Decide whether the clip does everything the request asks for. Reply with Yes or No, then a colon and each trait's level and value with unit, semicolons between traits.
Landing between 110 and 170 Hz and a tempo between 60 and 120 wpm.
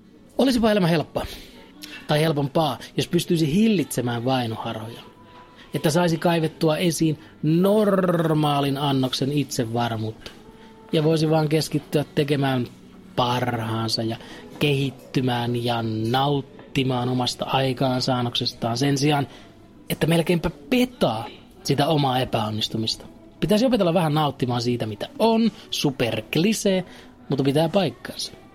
Yes: medium, 140 Hz; average, 100 wpm